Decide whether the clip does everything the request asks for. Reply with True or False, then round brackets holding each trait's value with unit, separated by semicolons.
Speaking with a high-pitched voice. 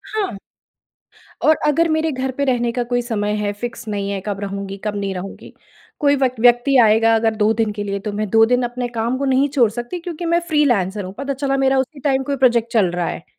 True (240 Hz)